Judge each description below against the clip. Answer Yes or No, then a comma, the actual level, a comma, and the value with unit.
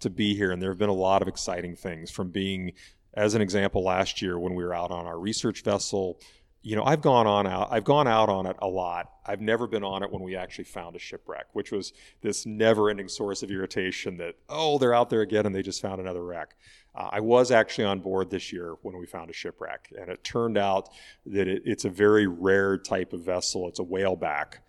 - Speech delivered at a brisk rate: Yes, fast, 245 wpm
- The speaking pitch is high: No, low, 100 Hz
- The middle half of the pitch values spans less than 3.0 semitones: Yes, narrow, 2.5 semitones